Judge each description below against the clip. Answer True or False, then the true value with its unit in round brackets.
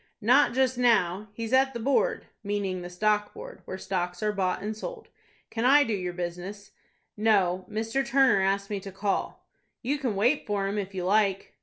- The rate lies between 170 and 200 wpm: True (185 wpm)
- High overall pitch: True (205 Hz)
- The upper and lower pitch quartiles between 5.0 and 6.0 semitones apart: False (3.7 semitones)